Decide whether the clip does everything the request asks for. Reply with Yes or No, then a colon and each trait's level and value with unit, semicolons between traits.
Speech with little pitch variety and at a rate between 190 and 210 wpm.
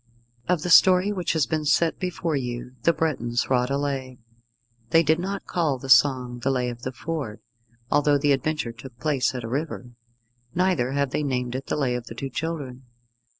No: average, 4.2 semitones; average, 195 wpm